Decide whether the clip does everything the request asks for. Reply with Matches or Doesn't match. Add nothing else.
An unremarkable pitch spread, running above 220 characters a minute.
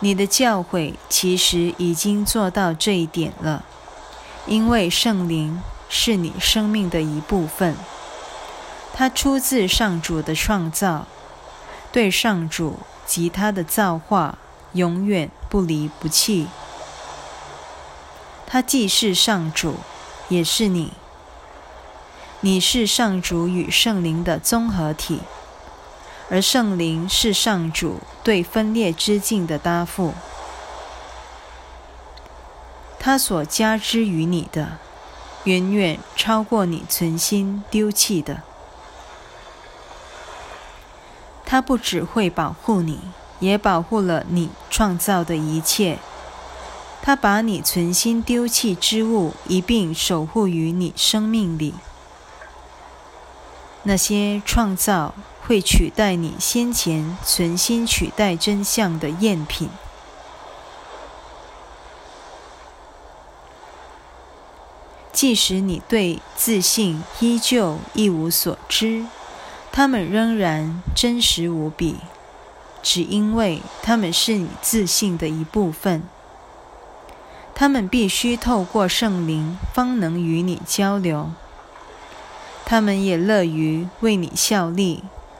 Doesn't match